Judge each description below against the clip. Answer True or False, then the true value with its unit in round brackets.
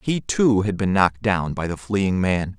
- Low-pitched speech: True (100 Hz)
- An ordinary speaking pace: False (230 wpm)